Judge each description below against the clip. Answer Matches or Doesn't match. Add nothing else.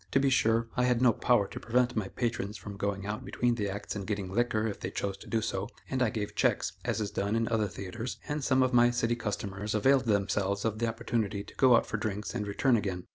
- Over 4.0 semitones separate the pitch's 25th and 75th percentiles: Doesn't match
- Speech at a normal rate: Doesn't match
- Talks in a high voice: Doesn't match